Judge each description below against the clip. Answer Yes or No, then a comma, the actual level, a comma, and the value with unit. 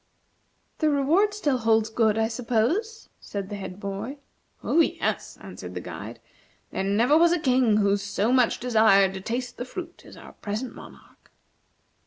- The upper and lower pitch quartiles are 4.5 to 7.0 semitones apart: Yes, wide, 5.5 semitones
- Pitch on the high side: Yes, high, 230 Hz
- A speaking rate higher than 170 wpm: No, average, 165 wpm